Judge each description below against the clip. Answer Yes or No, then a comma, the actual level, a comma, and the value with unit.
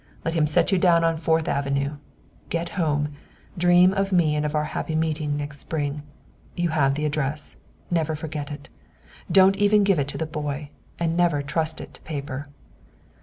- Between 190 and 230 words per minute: No, average, 180 wpm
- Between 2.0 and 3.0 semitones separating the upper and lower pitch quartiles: Yes, narrow, 2.6 semitones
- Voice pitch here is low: No, medium, 155 Hz